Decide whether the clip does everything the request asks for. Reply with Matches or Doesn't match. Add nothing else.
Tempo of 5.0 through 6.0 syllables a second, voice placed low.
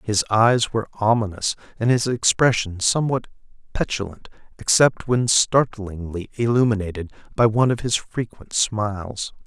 Doesn't match